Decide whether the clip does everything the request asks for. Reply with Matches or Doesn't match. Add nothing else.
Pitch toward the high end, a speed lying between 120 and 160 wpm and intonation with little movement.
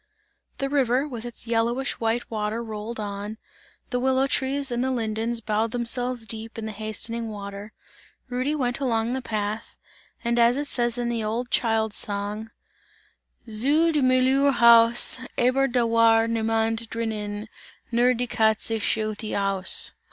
Matches